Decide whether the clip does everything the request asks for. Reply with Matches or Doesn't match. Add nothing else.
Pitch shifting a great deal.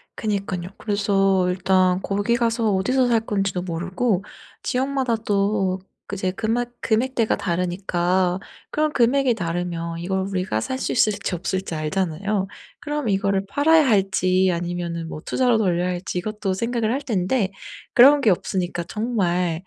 Doesn't match